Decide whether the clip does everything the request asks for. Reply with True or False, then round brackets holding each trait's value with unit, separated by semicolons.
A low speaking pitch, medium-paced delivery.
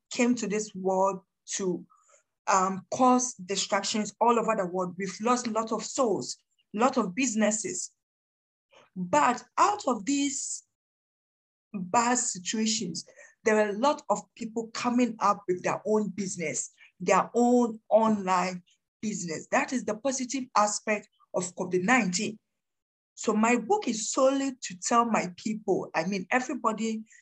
False (215 Hz; 140 wpm)